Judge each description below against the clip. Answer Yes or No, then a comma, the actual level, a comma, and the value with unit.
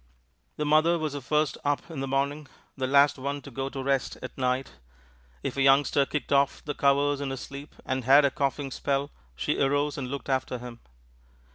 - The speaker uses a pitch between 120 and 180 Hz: Yes, medium, 140 Hz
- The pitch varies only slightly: Yes, narrow, 1.3 semitones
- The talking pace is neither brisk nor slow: No, fast, 210 wpm